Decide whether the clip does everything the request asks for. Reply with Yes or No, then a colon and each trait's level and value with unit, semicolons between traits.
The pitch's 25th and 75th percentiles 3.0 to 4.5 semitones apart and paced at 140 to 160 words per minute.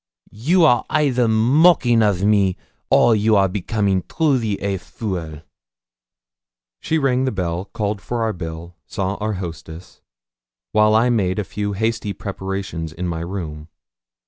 Yes: average, 3.9 semitones; average, 145 wpm